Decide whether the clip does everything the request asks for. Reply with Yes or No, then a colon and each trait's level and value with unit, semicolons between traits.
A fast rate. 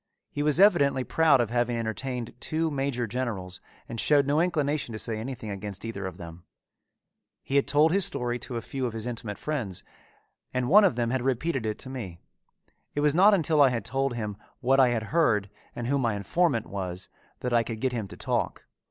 Yes: fast, 210 wpm